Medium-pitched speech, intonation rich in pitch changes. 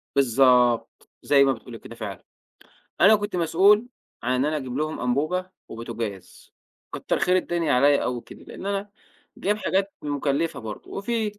Yes: medium, 145 Hz; wide, 7.5 semitones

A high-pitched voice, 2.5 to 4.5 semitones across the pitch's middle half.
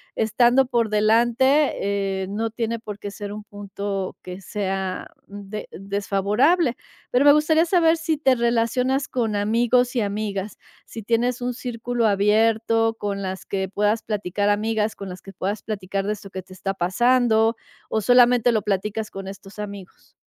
Yes: high, 215 Hz; average, 3.2 semitones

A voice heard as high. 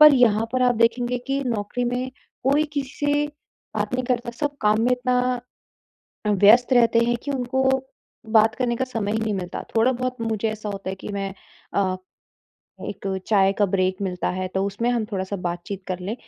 Yes: high, 230 Hz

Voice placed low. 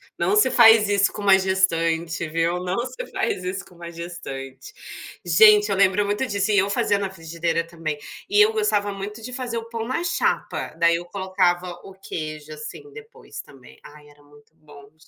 No: high, 190 Hz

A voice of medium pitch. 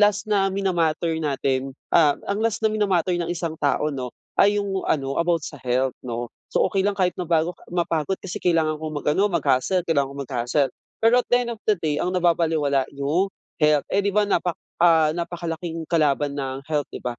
Yes: medium, 165 Hz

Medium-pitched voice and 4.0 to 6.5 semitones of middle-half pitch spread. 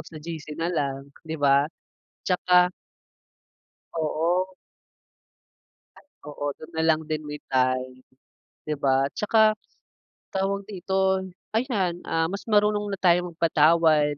Yes: medium, 165 Hz; average, 4.3 semitones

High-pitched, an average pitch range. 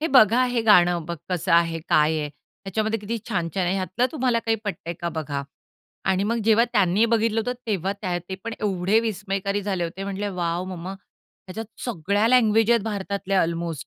Yes: high, 195 Hz; average, 4.0 semitones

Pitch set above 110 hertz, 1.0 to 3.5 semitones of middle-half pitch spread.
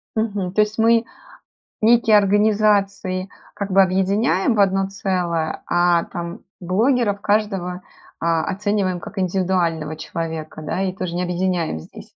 Yes: high, 190 Hz; average, 2.8 semitones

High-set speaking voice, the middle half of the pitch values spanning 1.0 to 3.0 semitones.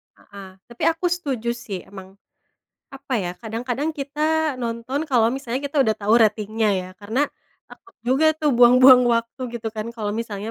No: high, 235 Hz; average, 3.9 semitones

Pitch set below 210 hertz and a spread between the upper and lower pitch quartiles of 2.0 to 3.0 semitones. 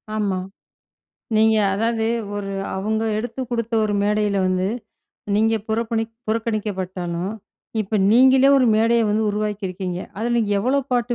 No: high, 220 Hz; narrow, 2.4 semitones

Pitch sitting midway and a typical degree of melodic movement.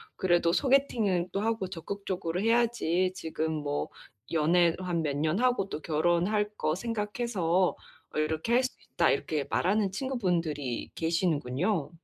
Yes: medium, 180 Hz; average, 4.7 semitones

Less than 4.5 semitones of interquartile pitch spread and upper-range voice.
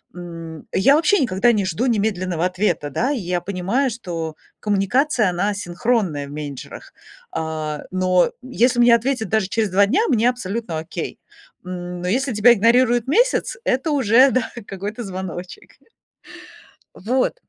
No: wide, 5.5 semitones; high, 205 Hz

